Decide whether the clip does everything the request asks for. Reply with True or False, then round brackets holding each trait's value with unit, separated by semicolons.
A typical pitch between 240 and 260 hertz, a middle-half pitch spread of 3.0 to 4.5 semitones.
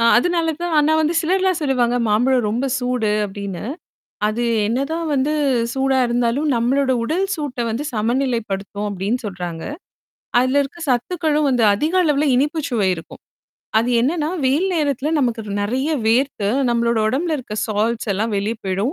False (250 Hz; 5.0 semitones)